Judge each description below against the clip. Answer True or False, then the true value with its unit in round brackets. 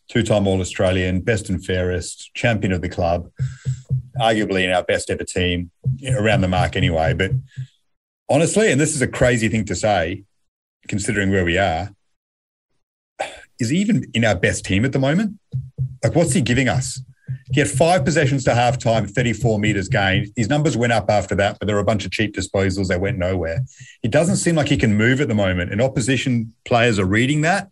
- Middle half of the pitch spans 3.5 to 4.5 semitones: False (5.1 semitones)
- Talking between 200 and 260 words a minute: True (205 wpm)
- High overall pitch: False (115 Hz)